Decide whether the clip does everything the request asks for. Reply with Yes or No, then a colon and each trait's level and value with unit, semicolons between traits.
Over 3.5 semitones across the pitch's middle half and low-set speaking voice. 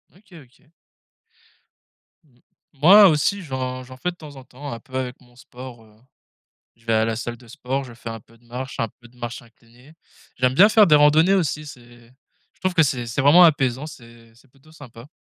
Yes: average, 3.9 semitones; low, 130 Hz